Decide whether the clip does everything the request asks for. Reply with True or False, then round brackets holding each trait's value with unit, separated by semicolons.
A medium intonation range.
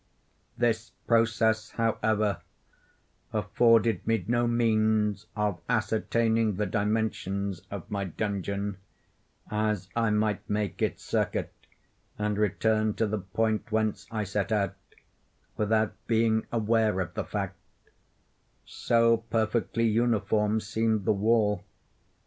False (1.5 semitones)